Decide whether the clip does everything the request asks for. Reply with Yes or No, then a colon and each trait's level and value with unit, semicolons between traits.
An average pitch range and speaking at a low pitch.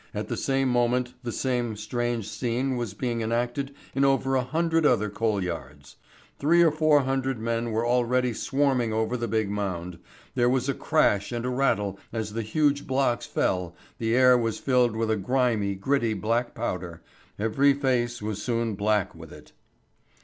Yes: average, 3.5 semitones; low, 120 Hz